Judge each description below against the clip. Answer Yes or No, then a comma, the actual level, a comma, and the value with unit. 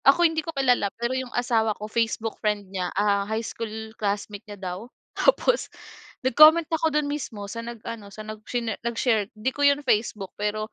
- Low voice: No, high, 225 Hz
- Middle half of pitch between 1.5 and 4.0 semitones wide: Yes, average, 3.7 semitones